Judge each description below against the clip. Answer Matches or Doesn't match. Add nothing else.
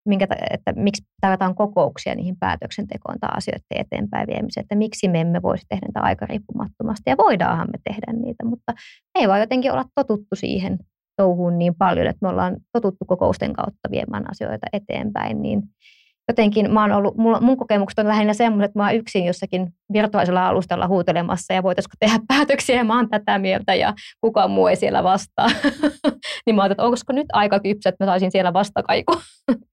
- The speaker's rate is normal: Doesn't match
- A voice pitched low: Doesn't match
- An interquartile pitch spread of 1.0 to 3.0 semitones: Doesn't match